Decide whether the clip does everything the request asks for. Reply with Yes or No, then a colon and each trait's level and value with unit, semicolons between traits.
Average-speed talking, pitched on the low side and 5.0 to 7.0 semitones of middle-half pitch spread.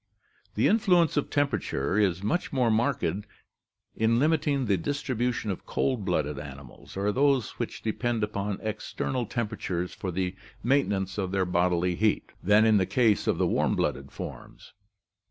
Yes: average, 155 wpm; low, 105 Hz; wide, 5.4 semitones